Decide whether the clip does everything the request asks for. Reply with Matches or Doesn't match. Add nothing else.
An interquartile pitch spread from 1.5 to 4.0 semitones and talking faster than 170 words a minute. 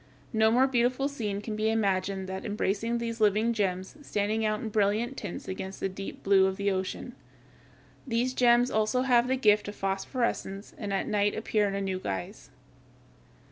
Matches